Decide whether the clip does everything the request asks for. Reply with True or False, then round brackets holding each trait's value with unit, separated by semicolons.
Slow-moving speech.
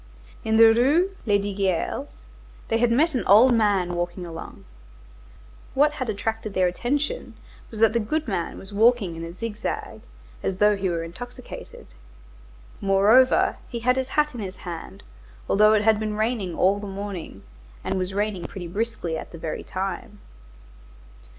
False (160 wpm)